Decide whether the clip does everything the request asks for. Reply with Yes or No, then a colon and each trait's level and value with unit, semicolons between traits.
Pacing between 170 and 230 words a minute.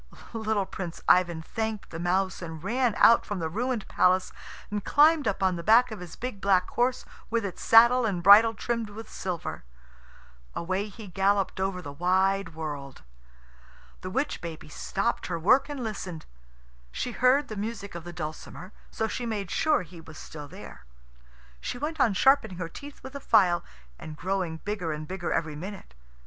Yes: average, 180 wpm